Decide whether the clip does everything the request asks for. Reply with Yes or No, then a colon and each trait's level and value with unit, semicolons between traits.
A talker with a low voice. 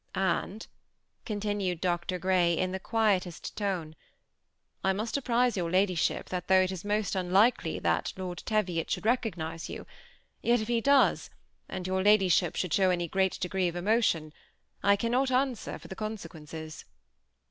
No: high, 190 Hz